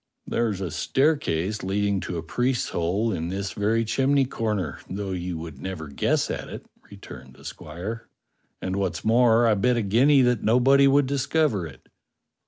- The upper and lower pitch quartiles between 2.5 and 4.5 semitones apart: No, average, 5.1 semitones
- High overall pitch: No, low, 105 Hz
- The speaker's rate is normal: Yes, average, 175 wpm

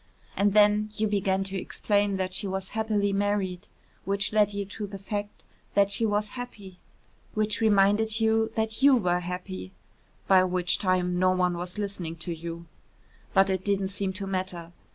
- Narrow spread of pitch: Yes, narrow, 2.1 semitones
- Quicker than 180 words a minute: No, average, 175 wpm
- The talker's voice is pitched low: No, high, 195 Hz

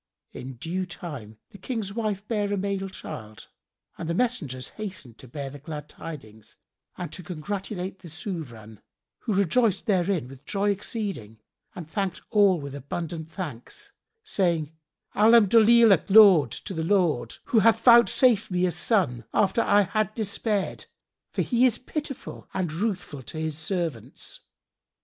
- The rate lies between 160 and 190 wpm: No, average, 140 wpm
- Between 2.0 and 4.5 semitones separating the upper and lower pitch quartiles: No, wide, 5.6 semitones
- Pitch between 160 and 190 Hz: Yes, medium, 185 Hz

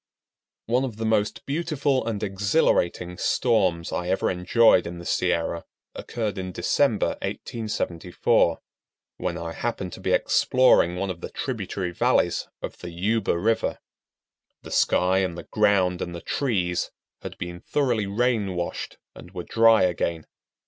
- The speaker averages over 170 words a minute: No, average, 145 wpm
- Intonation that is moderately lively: Yes, average, 4.5 semitones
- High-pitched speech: No, very low, 95 Hz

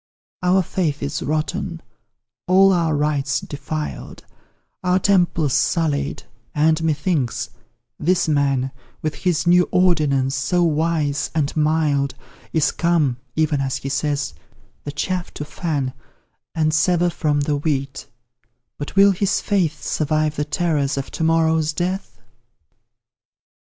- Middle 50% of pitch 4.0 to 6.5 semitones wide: No, average, 3.2 semitones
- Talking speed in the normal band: No, slow, 125 wpm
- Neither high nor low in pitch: Yes, medium, 155 Hz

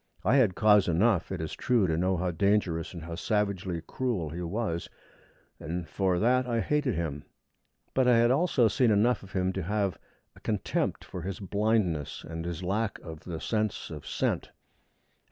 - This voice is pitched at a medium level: No, very low, 95 Hz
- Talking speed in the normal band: Yes, average, 180 wpm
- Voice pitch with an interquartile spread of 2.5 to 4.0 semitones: No, average, 4.9 semitones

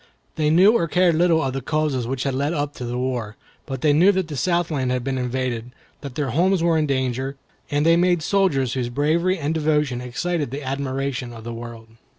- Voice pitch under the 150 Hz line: Yes, medium, 140 Hz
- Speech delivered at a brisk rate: Yes, fast, 215 wpm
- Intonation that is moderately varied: Yes, average, 4.2 semitones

